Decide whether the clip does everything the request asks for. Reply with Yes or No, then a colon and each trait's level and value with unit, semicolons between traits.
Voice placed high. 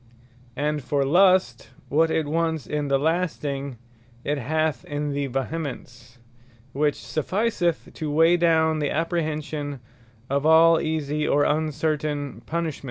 No: medium, 150 Hz